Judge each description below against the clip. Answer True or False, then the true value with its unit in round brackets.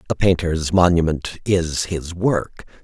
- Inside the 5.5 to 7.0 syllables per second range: False (3.7 syllables/s)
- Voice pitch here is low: True (85 Hz)